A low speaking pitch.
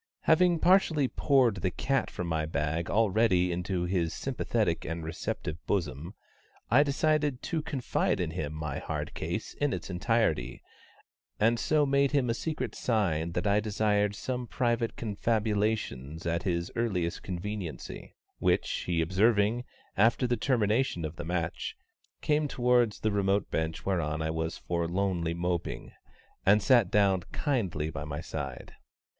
Yes: low, 100 Hz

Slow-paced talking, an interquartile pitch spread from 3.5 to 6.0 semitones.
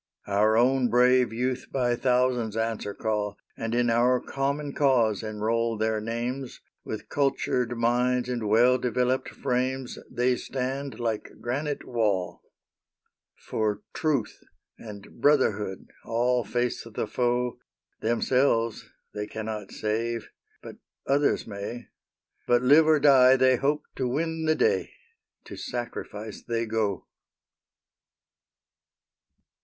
No: slow, 115 wpm; narrow, 2.6 semitones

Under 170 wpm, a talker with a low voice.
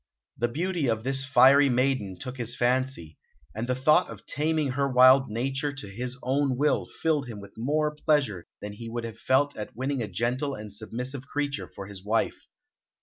No: average, 190 wpm; low, 130 Hz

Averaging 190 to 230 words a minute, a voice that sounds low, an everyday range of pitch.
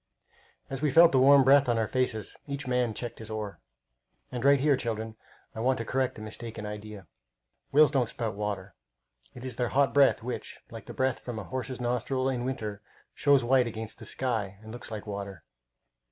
Yes: average, 195 wpm; low, 120 Hz; average, 3.4 semitones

